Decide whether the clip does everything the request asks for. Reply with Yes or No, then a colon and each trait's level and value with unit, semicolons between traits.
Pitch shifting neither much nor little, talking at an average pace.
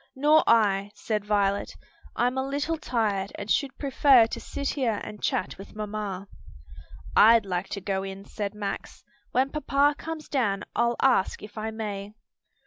Yes: average, 4.9 semitones; average, 160 wpm